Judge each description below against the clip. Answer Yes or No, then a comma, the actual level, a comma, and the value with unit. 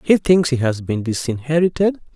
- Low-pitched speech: No, medium, 145 Hz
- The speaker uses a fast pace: No, average, 165 wpm